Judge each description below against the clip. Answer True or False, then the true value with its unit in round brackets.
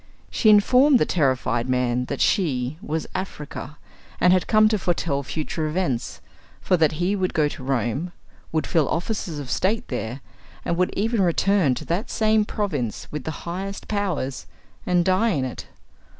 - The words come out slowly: False (165 wpm)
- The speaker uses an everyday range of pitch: False (6.1 semitones)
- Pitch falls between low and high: True (170 Hz)